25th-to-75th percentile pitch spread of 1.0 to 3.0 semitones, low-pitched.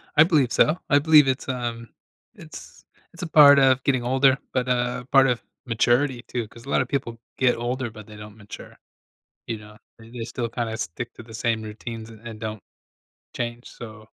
Yes: average, 2.7 semitones; low, 120 Hz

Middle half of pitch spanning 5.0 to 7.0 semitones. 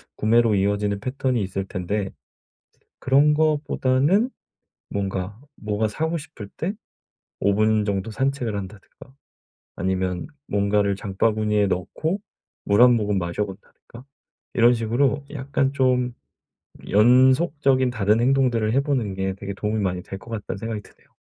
No: average, 4.5 semitones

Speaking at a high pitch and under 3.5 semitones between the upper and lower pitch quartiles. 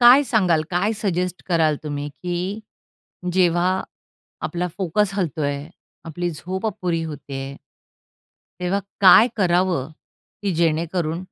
No: medium, 175 Hz; average, 3.0 semitones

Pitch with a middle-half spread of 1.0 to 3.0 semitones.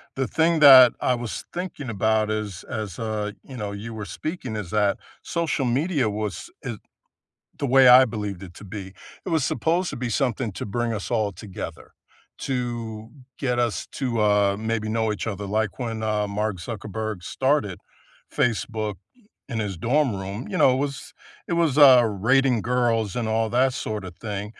No: average, 3.6 semitones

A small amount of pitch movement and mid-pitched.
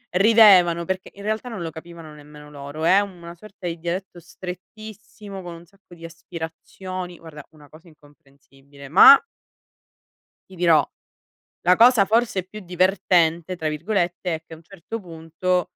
No: average, 3.0 semitones; medium, 175 Hz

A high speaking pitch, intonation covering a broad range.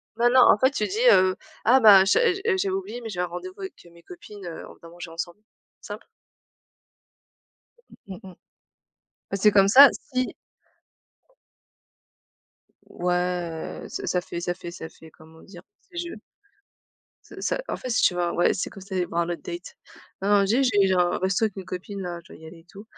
Yes: high, 195 Hz; wide, 5.7 semitones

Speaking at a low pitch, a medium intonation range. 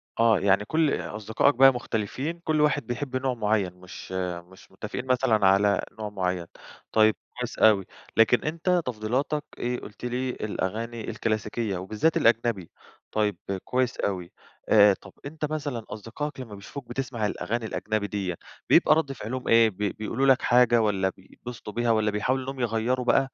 Yes: low, 115 Hz; average, 3.7 semitones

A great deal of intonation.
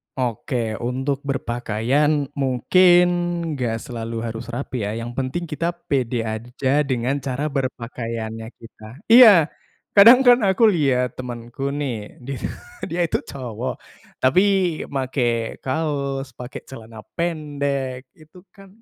No: average, 4.0 semitones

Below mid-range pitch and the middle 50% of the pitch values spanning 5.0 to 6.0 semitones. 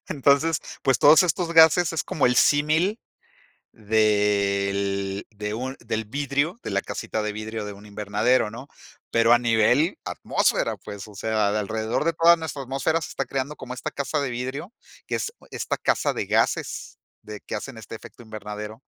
Yes: low, 120 Hz; wide, 5.5 semitones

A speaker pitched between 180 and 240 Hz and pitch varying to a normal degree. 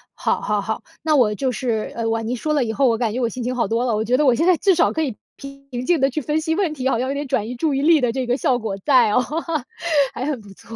No: very high, 255 Hz; average, 3.8 semitones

